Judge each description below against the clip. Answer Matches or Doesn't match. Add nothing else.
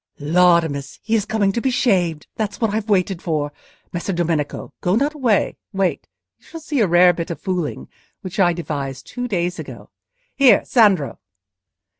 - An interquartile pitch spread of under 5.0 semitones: Matches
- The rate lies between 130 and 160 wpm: Doesn't match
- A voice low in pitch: Doesn't match